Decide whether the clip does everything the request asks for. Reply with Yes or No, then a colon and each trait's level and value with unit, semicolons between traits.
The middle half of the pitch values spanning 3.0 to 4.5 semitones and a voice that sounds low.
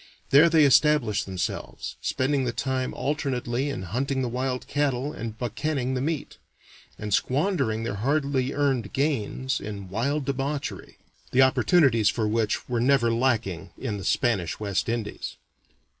Yes: average, 3.9 semitones; low, 130 Hz